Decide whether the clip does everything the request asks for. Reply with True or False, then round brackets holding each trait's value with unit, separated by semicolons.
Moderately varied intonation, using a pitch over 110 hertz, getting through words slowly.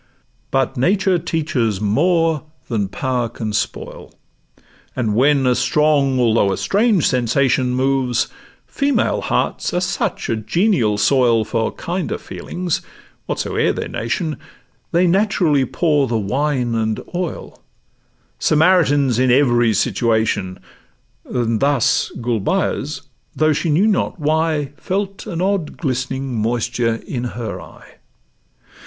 False (6.0 semitones; 135 Hz; 115 wpm)